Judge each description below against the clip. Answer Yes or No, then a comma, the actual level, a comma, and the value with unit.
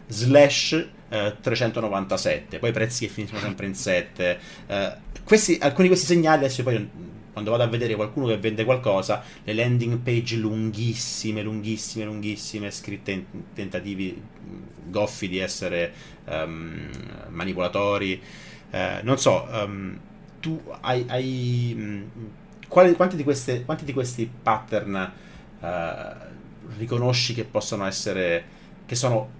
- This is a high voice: No, low, 110 Hz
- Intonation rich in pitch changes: No, average, 3.5 semitones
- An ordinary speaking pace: Yes, average, 125 wpm